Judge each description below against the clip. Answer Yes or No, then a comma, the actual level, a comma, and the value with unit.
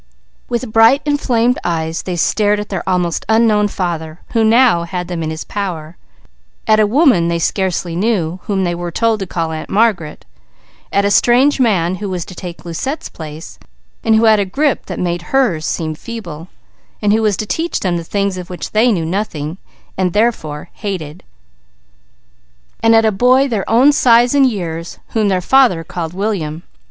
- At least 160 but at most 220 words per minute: Yes, average, 185 wpm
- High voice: Yes, high, 195 Hz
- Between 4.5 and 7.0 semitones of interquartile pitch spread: Yes, average, 5.0 semitones